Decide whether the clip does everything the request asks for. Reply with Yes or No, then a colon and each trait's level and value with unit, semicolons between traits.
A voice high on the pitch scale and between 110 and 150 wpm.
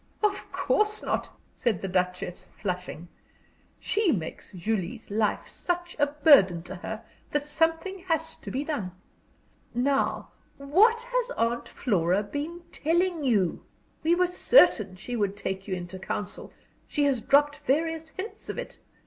Yes: very high, 275 Hz; average, 145 wpm